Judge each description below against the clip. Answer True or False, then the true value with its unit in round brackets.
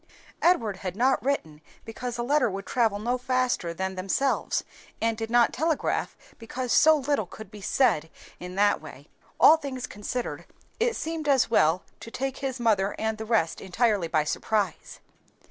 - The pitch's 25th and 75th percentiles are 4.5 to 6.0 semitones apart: True (4.8 semitones)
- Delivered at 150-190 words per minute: True (165 wpm)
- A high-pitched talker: True (230 Hz)